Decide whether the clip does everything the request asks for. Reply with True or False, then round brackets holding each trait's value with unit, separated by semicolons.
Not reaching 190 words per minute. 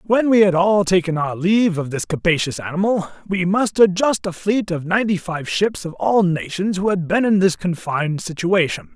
False (200 wpm)